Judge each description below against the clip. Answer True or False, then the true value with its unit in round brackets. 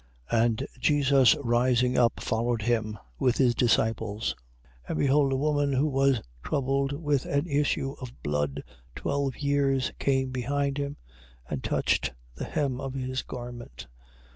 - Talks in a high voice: False (130 Hz)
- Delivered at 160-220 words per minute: False (145 wpm)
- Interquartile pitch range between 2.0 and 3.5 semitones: True (3.0 semitones)